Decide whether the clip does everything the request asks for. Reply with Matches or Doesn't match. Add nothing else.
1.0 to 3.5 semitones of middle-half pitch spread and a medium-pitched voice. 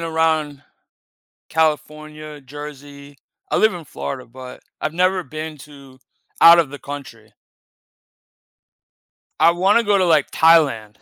Matches